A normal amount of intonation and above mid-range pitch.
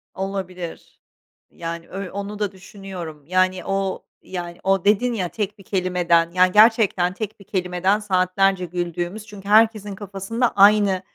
No: narrow, 2.2 semitones; high, 195 Hz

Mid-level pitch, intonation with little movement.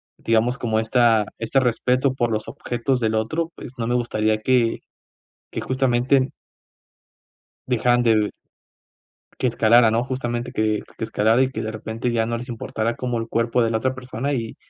No: low, 120 Hz; narrow, 2.0 semitones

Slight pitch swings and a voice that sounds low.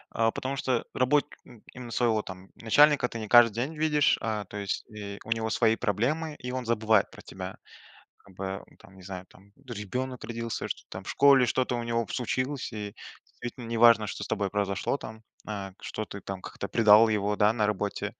No: average, 3.4 semitones; low, 115 Hz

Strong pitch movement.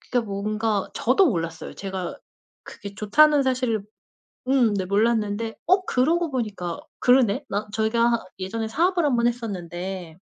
No: average, 4.4 semitones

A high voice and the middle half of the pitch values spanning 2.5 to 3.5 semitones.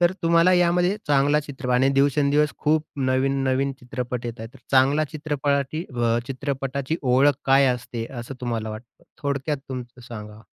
No: low, 135 Hz; average, 2.8 semitones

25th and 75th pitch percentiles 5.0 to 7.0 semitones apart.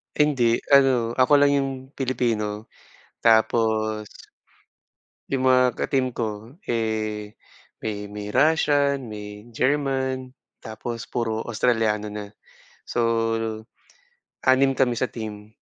No: average, 3.3 semitones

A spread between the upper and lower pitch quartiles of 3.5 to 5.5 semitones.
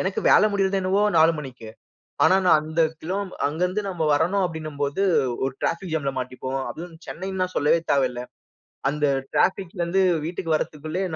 Yes: average, 4.2 semitones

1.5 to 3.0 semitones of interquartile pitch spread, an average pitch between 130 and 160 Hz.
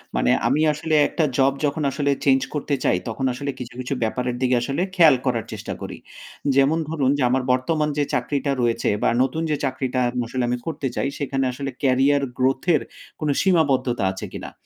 Yes: narrow, 2.5 semitones; low, 135 Hz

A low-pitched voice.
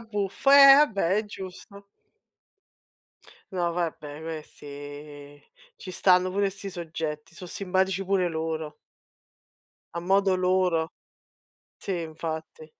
No: medium, 180 Hz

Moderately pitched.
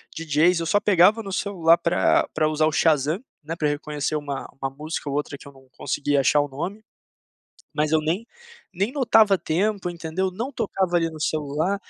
Yes: medium, 165 Hz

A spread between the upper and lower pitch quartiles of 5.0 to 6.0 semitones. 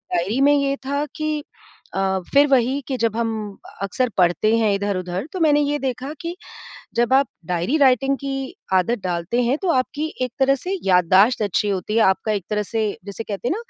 Yes: wide, 5.6 semitones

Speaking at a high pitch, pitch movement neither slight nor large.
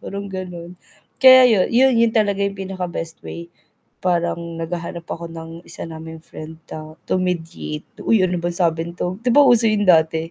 No: medium, 175 Hz; average, 3.3 semitones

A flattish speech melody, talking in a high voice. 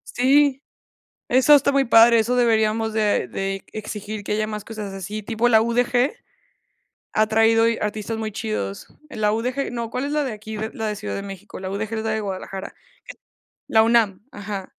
Yes: narrow, 2.2 semitones; high, 220 Hz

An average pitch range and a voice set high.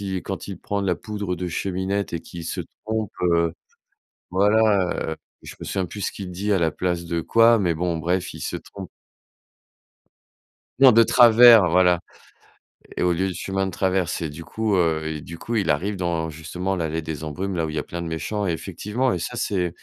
No: average, 3.2 semitones; very low, 90 Hz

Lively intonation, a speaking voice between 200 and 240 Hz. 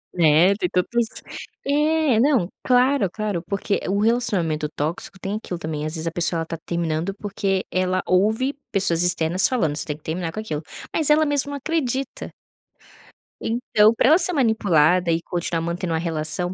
No: wide, 6.3 semitones; medium, 185 Hz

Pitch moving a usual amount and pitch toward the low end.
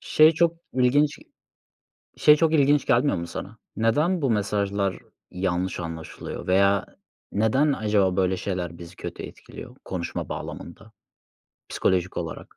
No: wide, 7.5 semitones; low, 100 Hz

